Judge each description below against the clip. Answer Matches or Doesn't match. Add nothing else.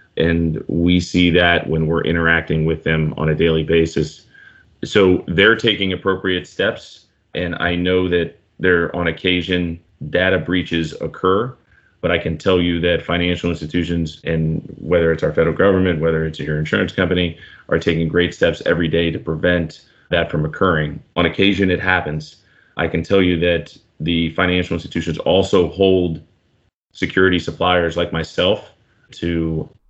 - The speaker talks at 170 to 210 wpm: Doesn't match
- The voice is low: Matches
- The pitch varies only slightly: Matches